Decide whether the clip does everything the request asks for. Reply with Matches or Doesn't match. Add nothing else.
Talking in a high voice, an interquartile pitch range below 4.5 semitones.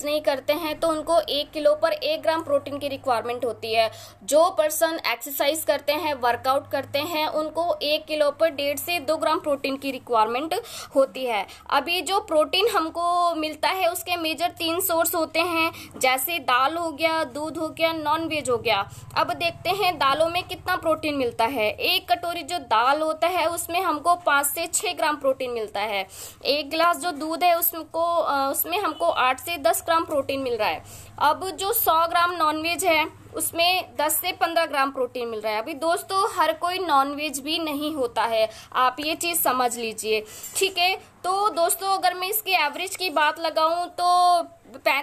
Matches